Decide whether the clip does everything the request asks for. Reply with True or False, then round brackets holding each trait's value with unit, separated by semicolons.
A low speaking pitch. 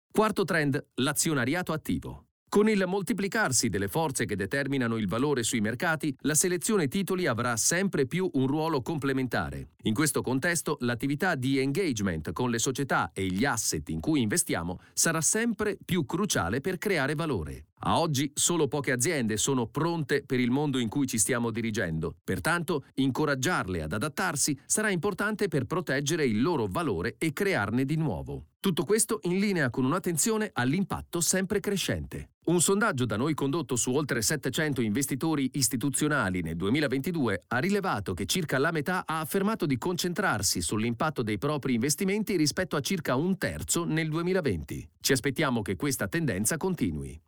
False (145 Hz)